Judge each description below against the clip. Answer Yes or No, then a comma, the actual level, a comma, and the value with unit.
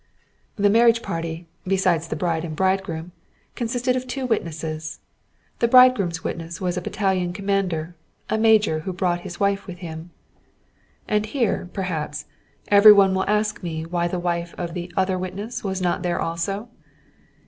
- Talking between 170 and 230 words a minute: No, average, 160 wpm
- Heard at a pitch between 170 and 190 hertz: Yes, medium, 185 Hz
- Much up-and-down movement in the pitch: No, average, 3.4 semitones